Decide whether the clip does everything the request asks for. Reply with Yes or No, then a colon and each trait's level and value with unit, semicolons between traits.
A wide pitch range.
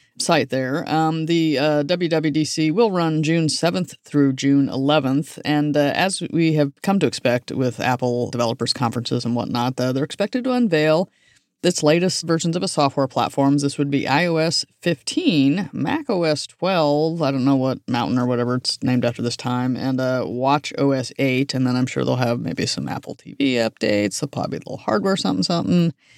No: average, 4.3 semitones